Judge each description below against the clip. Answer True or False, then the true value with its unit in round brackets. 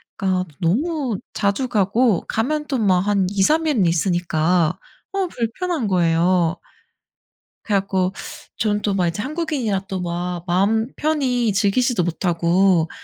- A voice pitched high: True (195 Hz)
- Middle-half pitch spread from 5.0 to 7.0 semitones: True (5.5 semitones)